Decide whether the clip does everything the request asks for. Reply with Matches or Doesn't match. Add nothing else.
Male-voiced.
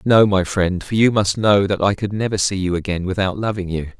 Matches